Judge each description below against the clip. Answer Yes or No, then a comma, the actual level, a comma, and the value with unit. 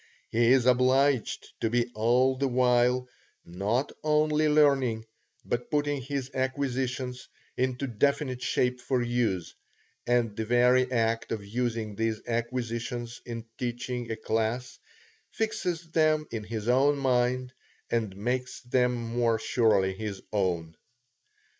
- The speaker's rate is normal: No, slow, 125 wpm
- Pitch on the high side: No, low, 125 Hz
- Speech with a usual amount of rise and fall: No, narrow, 2.3 semitones